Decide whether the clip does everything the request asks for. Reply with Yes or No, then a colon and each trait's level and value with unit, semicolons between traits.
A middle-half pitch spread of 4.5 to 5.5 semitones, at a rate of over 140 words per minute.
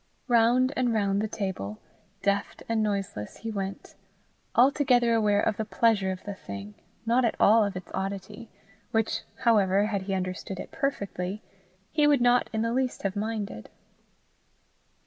No: average, 3.2 semitones; average, 155 wpm